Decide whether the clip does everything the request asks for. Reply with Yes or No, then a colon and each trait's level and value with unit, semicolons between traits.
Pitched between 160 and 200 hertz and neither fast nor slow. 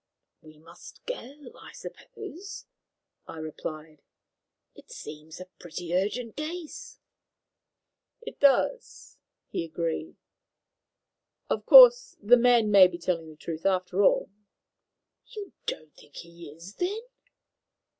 No: high, 190 Hz; slow, 115 wpm